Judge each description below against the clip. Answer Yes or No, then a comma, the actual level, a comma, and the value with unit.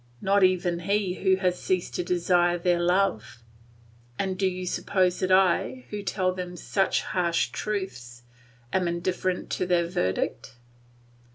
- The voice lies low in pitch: No, medium, 180 Hz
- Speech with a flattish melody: Yes, narrow, 1.5 semitones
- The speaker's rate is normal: Yes, average, 145 wpm